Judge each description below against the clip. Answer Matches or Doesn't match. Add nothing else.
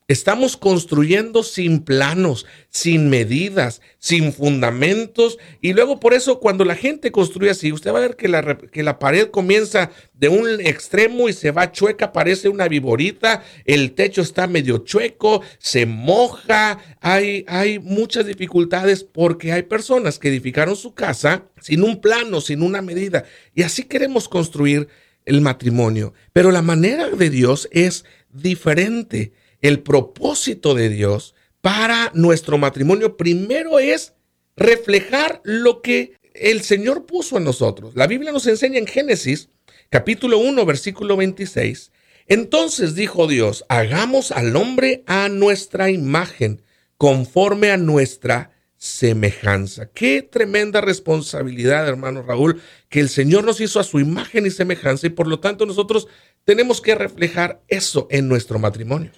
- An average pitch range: Doesn't match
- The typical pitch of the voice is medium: Matches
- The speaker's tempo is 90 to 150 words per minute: Matches